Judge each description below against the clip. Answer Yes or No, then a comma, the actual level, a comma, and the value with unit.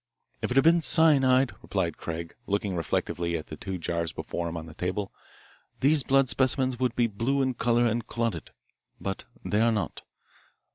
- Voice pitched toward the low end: Yes, low, 115 Hz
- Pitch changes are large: Yes, wide, 6.6 semitones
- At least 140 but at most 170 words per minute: No, average, 180 wpm